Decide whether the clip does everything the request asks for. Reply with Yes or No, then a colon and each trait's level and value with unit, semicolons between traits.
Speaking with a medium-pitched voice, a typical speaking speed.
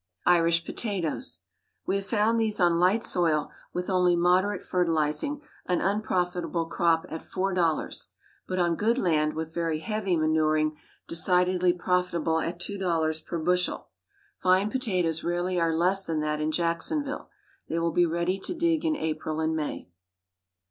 Yes: medium, 175 Hz; average, 155 wpm